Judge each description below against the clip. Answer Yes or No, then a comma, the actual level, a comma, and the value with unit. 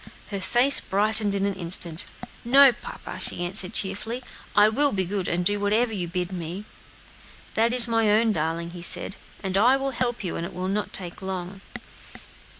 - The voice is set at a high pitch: Yes, high, 200 Hz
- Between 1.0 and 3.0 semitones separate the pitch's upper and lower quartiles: No, average, 3.9 semitones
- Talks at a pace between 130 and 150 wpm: No, average, 185 wpm